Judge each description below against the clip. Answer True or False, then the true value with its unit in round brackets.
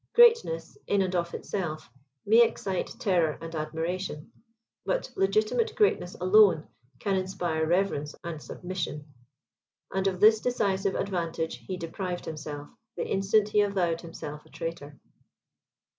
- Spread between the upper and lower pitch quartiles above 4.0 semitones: False (3.7 semitones)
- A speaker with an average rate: False (130 wpm)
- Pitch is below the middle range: False (185 Hz)